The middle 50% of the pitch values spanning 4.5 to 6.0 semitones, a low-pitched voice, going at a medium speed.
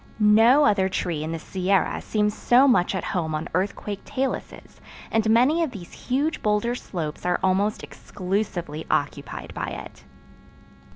No: average, 4.9 semitones; high, 200 Hz; average, 150 wpm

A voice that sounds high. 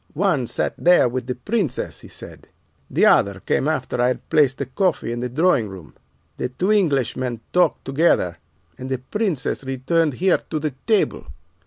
No: low, 135 Hz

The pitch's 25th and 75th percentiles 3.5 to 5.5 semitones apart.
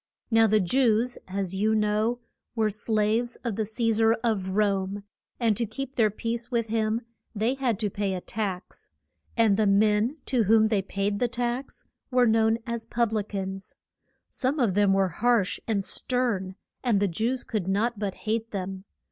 No: average, 2.8 semitones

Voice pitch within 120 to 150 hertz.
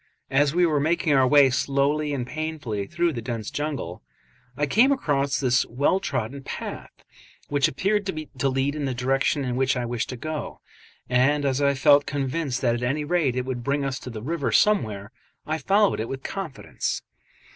Yes: medium, 140 Hz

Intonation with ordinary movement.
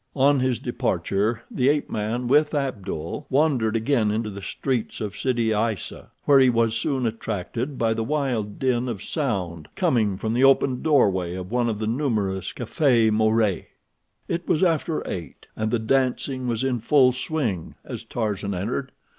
Yes: average, 3.9 semitones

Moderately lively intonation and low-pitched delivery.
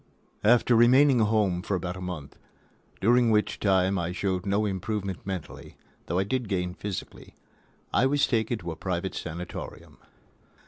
Yes: average, 3.7 semitones; low, 100 Hz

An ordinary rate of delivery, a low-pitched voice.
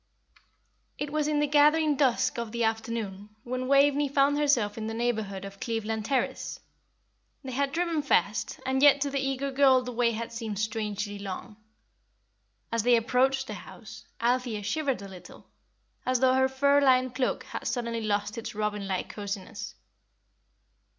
No: average, 165 wpm; high, 245 Hz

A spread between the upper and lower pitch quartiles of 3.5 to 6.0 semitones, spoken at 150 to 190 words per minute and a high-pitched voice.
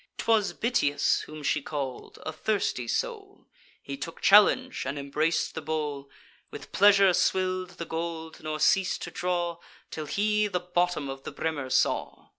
No: average, 4.2 semitones; average, 160 wpm; medium, 165 Hz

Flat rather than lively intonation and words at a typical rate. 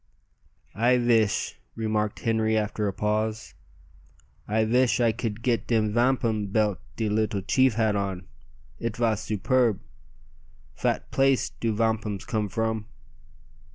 No: narrow, 1.6 semitones; slow, 125 wpm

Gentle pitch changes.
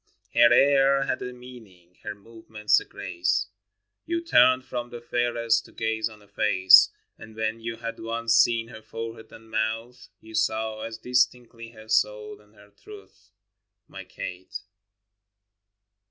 Yes: narrow, 1.9 semitones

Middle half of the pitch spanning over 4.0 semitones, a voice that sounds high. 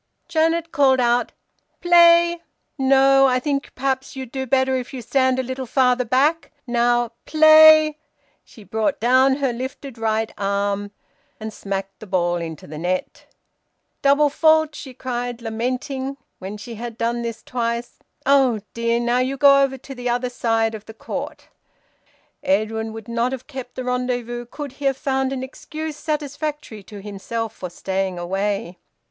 No: average, 3.5 semitones; very high, 250 Hz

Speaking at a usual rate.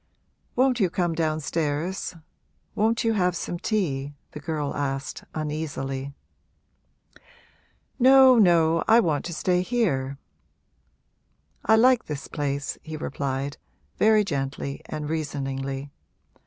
No: slow, 110 wpm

